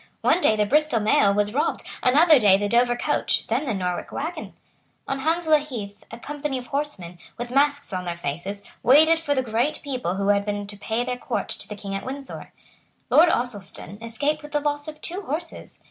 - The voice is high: Yes, very high, 250 Hz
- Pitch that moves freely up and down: Yes, wide, 6.4 semitones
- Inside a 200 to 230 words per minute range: Yes, fast, 205 wpm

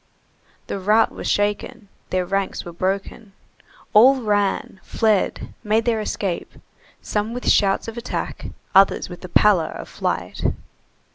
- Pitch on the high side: Yes, high, 205 Hz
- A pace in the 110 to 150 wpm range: Yes, slow, 135 wpm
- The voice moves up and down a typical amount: No, narrow, 2.3 semitones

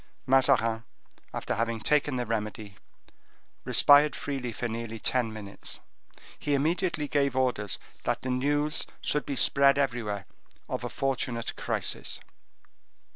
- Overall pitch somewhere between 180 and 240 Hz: No, low, 125 Hz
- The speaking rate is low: Yes, slow, 125 wpm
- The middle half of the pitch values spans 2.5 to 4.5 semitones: Yes, average, 3.9 semitones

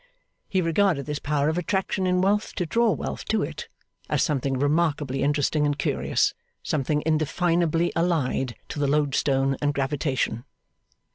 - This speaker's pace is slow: No, average, 145 wpm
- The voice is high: No, medium, 150 Hz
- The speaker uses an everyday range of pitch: Yes, average, 3.6 semitones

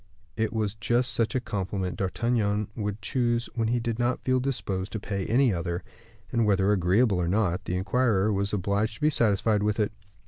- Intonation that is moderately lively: Yes, average, 3.2 semitones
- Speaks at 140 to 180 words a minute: No, average, 195 wpm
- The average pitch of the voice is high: No, low, 105 Hz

